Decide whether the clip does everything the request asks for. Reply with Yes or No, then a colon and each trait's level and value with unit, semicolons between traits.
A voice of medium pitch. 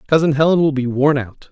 Yes: medium, 145 Hz